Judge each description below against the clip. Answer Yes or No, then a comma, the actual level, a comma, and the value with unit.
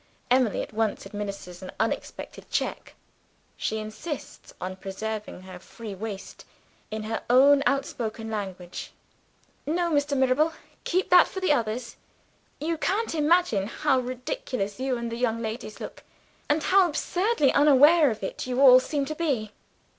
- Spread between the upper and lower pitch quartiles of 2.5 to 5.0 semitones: No, wide, 5.6 semitones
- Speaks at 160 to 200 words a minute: No, average, 145 wpm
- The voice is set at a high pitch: Yes, very high, 250 Hz